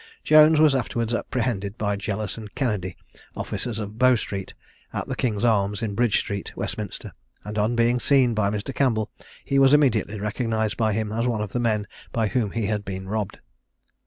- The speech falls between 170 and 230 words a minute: Yes, average, 190 wpm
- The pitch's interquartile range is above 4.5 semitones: No, average, 2.8 semitones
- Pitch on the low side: Yes, low, 110 Hz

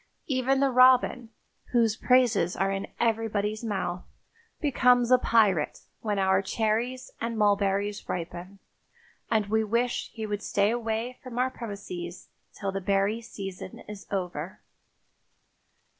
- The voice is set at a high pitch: Yes, high, 215 Hz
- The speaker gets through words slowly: Yes, slow, 130 wpm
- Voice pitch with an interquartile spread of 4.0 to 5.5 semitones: No, average, 3.4 semitones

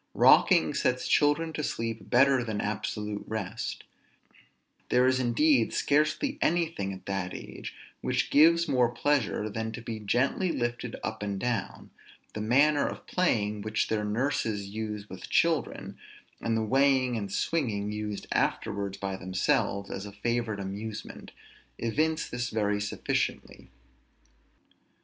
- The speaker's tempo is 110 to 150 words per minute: Yes, slow, 135 wpm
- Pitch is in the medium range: No, low, 115 Hz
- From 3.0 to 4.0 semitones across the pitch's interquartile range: No, average, 4.7 semitones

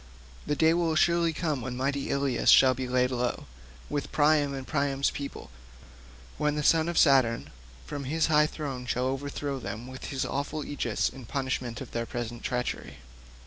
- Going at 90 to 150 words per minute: No, average, 175 wpm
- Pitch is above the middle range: No, medium, 140 Hz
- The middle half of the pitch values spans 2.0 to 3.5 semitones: Yes, average, 2.9 semitones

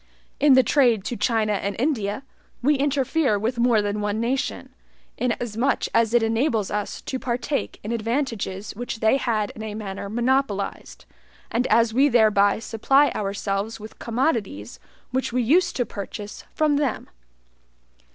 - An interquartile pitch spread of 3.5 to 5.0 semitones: Yes, average, 3.9 semitones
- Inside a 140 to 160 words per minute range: Yes, average, 150 wpm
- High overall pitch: Yes, high, 230 Hz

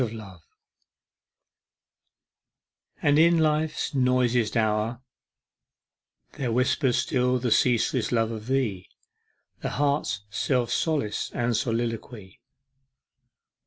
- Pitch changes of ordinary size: Yes, average, 3.1 semitones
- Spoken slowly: Yes, slow, 90 wpm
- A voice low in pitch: Yes, low, 120 Hz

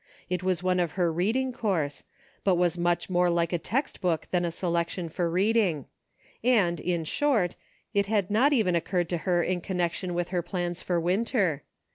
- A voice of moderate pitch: Yes, medium, 180 Hz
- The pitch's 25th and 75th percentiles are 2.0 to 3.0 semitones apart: Yes, narrow, 2.5 semitones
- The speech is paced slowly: No, average, 190 wpm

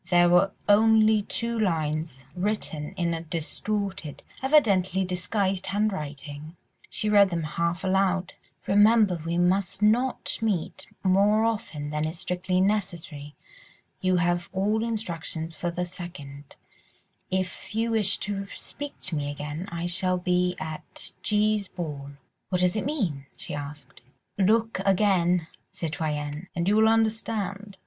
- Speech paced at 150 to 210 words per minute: No, slow, 135 wpm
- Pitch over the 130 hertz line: Yes, medium, 185 Hz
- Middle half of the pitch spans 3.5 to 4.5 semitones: Yes, average, 4.0 semitones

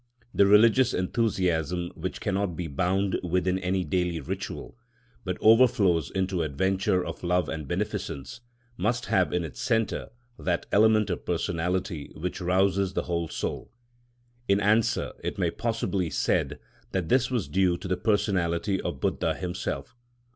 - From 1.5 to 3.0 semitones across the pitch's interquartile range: Yes, average, 2.7 semitones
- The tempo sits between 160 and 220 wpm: No, average, 145 wpm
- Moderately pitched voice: No, very low, 95 Hz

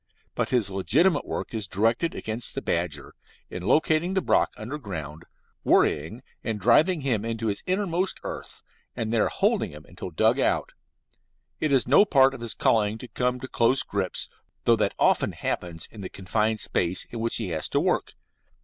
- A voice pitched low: Yes, low, 115 Hz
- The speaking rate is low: No, average, 180 wpm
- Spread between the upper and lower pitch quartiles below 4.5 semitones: No, wide, 5.6 semitones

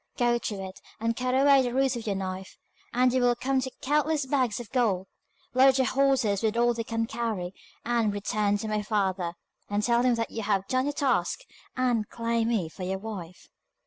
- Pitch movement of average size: Yes, average, 3.8 semitones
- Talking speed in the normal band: No, fast, 210 wpm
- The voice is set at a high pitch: Yes, high, 230 Hz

